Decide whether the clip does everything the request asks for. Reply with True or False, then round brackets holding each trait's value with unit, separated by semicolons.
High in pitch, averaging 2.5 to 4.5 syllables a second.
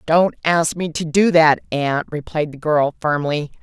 False (155 Hz; 4.1 syllables/s)